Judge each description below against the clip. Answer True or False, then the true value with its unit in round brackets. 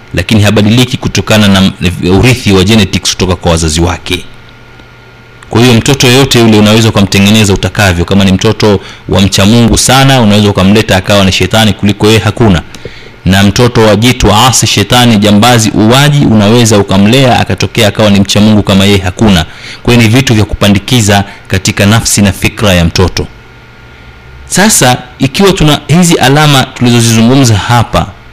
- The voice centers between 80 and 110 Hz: True (105 Hz)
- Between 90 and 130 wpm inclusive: False (140 wpm)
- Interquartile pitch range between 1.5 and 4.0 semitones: True (3.5 semitones)